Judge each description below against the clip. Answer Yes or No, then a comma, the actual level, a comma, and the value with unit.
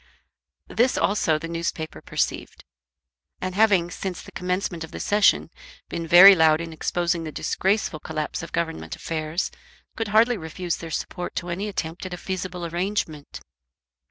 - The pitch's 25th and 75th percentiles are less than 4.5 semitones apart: Yes, average, 2.9 semitones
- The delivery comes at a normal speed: Yes, average, 155 wpm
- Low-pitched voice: No, medium, 175 Hz